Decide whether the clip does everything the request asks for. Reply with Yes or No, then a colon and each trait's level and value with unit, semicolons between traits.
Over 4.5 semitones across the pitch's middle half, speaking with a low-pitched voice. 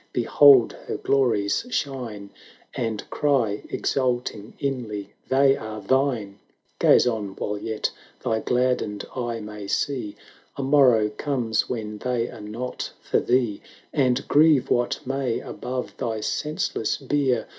No: average, 3.9 semitones; low, 120 Hz